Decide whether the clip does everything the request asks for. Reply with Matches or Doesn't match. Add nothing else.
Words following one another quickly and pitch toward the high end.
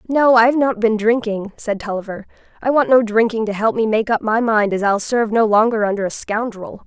Matches